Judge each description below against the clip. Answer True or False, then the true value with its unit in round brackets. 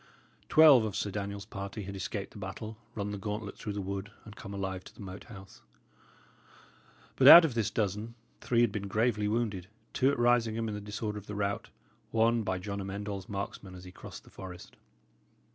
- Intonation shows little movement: True (2.3 semitones)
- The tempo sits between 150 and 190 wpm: False (200 wpm)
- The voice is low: True (105 Hz)